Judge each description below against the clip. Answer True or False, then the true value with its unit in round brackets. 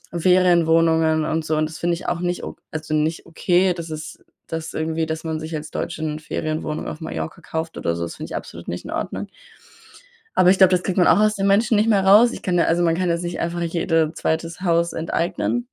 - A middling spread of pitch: False (2.2 semitones)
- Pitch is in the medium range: True (165 Hz)